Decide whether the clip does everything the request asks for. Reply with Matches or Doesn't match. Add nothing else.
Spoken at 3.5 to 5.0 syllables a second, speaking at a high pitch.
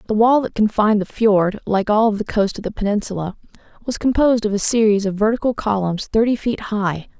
Doesn't match